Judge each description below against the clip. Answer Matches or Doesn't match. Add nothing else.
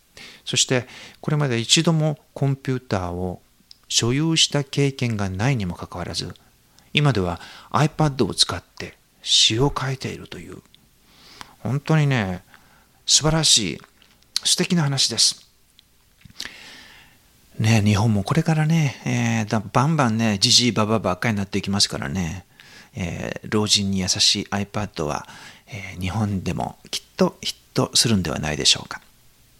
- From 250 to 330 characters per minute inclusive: Matches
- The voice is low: Matches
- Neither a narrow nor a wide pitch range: Doesn't match